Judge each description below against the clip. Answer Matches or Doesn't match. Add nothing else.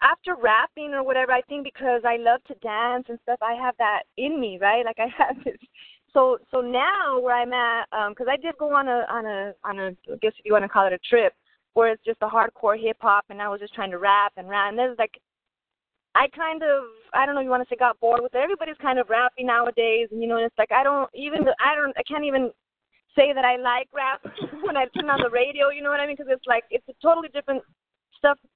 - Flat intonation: Doesn't match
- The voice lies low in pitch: Doesn't match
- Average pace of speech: Doesn't match